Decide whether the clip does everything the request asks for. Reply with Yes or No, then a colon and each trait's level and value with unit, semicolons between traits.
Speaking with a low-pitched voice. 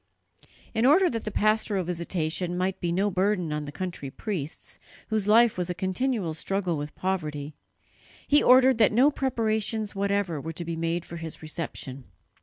No: medium, 185 Hz